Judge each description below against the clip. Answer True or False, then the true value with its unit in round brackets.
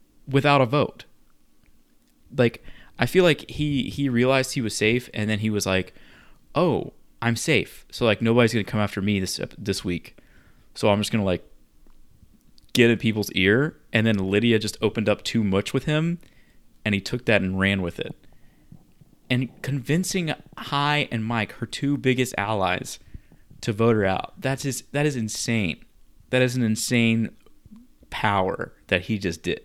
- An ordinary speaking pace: True (175 wpm)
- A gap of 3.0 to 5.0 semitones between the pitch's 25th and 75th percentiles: True (4.6 semitones)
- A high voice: False (115 Hz)